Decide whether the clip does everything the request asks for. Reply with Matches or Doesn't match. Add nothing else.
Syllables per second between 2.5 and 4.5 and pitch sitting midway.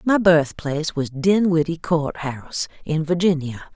Matches